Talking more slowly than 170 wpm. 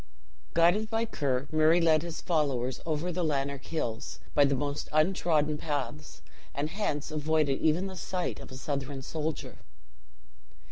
Yes: average, 145 wpm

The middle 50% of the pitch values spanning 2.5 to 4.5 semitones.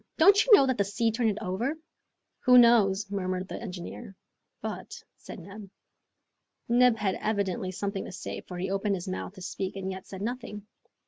Yes: average, 3.7 semitones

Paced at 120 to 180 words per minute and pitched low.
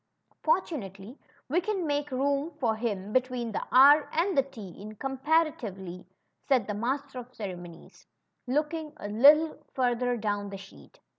No: average, 150 wpm; very high, 255 Hz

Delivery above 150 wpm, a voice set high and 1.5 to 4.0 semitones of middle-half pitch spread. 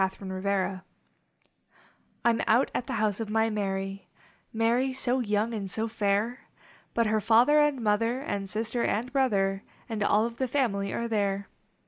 Yes: average, 160 wpm; high, 220 Hz; average, 2.9 semitones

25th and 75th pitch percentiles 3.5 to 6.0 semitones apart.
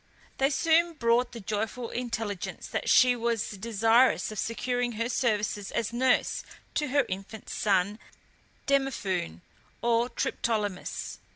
No: average, 3.1 semitones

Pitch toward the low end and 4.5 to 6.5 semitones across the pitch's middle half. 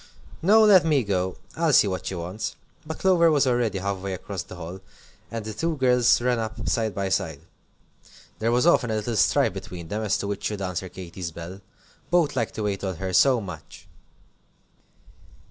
Yes: low, 105 Hz; average, 5.1 semitones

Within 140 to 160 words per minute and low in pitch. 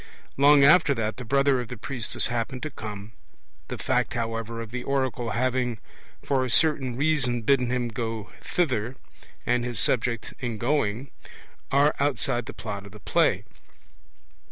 Yes: average, 155 wpm; low, 125 Hz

